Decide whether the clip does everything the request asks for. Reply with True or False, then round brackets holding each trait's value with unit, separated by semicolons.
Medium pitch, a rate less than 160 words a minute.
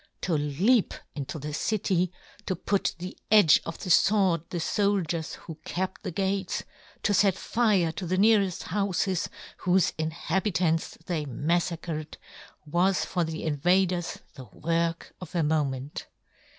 True (175 Hz; 140 wpm)